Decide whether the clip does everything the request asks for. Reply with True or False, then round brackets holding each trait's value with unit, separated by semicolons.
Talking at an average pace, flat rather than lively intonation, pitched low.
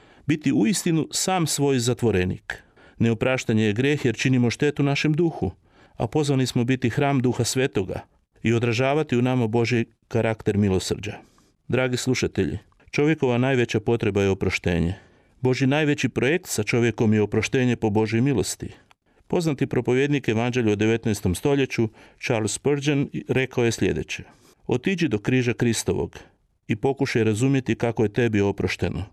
False (140 wpm; 3.7 semitones; 120 Hz)